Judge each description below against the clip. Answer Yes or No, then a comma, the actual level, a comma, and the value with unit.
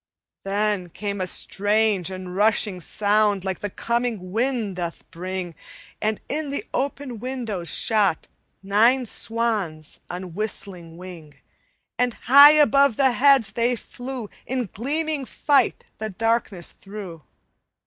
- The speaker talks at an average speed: No, slow, 125 wpm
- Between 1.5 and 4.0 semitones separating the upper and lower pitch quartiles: No, average, 4.9 semitones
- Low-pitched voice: No, high, 215 Hz